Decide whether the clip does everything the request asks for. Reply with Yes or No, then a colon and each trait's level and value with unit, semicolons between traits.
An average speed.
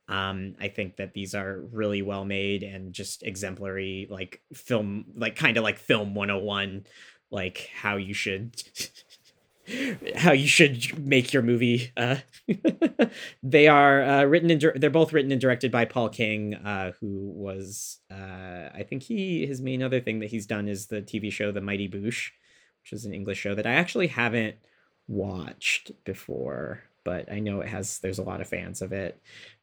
Yes: average, 180 wpm